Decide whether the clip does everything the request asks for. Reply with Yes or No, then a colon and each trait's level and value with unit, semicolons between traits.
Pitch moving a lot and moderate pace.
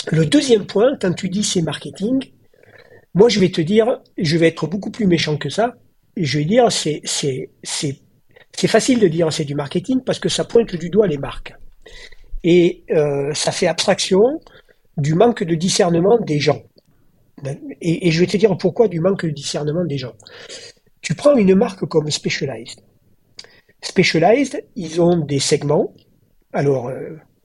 Yes: wide, 6.5 semitones; average, 175 wpm